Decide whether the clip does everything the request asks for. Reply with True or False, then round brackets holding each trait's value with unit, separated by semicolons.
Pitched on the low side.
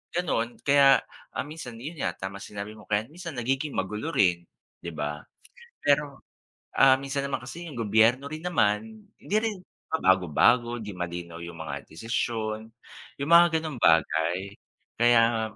True (115 Hz)